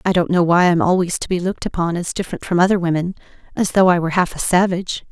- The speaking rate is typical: No, fast, 245 wpm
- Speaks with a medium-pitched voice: Yes, medium, 175 Hz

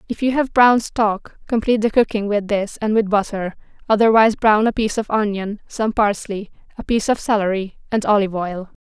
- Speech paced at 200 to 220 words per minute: No, average, 190 wpm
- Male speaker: No, female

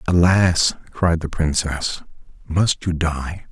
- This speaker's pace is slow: Yes, slow, 120 wpm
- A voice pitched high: No, very low, 85 Hz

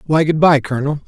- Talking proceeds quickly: Yes, fast, 225 wpm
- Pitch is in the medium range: Yes, medium, 150 Hz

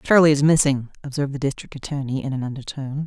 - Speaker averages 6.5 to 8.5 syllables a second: Yes, 7.1 syllables/s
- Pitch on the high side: No, medium, 140 Hz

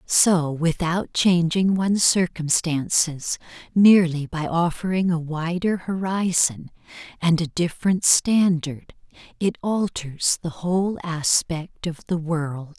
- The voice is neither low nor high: Yes, medium, 170 Hz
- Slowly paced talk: Yes, slow, 110 wpm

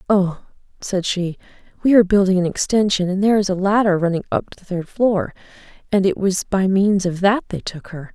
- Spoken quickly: Yes, fast, 215 wpm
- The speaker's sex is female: Yes, female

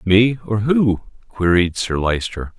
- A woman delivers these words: No, male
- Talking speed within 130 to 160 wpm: Yes, average, 140 wpm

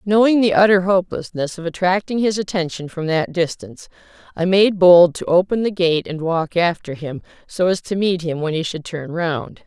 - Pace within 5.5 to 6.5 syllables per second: No, 5.1 syllables/s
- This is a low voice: No, medium, 180 Hz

